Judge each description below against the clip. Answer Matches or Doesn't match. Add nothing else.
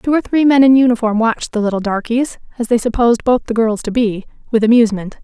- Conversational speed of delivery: Doesn't match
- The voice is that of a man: Doesn't match